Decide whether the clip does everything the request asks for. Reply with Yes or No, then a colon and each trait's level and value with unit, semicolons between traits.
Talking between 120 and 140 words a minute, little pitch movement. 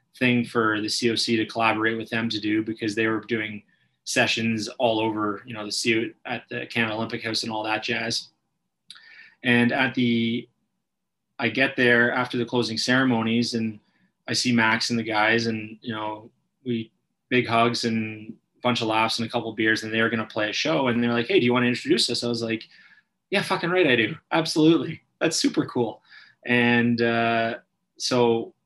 No: fast, 205 wpm; narrow, 1.4 semitones